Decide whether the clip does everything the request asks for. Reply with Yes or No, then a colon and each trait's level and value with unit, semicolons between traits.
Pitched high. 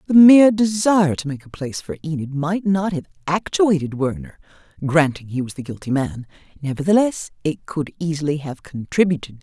No: medium, 160 Hz